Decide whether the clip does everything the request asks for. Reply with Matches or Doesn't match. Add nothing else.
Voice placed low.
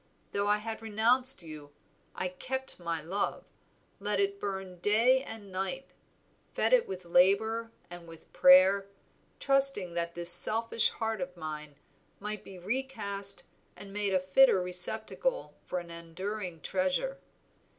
Doesn't match